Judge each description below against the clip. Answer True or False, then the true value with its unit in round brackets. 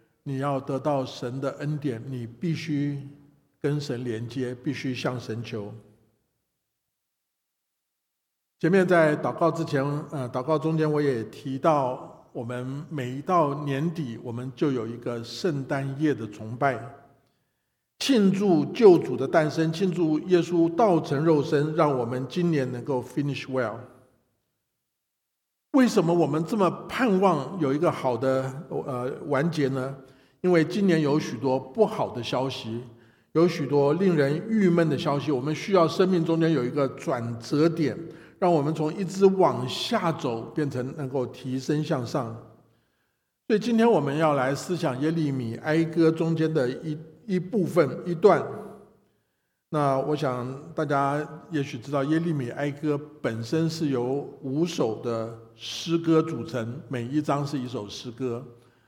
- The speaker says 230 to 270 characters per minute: False (220 characters per minute)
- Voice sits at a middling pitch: True (145 Hz)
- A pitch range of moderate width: True (4.1 semitones)